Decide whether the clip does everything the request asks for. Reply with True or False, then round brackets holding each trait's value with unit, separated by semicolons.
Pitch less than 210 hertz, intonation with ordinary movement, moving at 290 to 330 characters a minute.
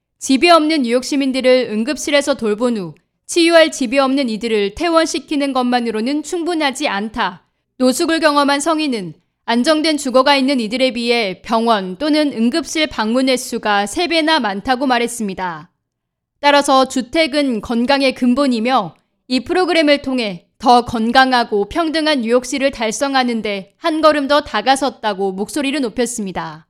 False (260 Hz; 4.2 semitones; 325 characters per minute)